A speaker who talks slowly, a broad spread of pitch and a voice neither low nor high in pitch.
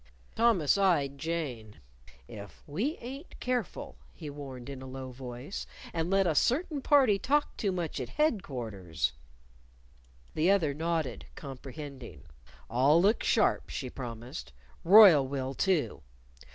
Yes: slow, 130 wpm; wide, 7.7 semitones; medium, 145 Hz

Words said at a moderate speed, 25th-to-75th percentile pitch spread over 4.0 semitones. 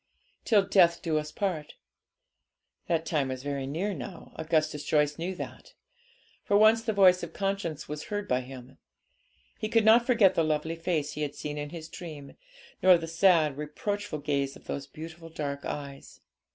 Yes: average, 175 wpm; average, 4.5 semitones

